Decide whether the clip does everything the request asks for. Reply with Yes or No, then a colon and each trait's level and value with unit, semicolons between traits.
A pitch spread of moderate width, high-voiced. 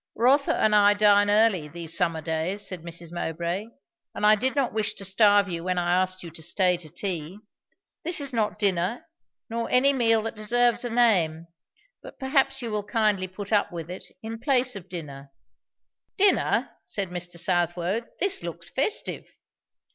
Yes: average, 4.8 semitones; high, 200 Hz